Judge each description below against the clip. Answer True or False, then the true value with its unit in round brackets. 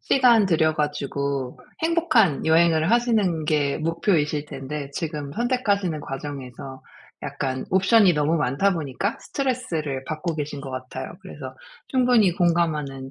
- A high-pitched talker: False (155 Hz)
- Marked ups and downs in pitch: True (5.9 semitones)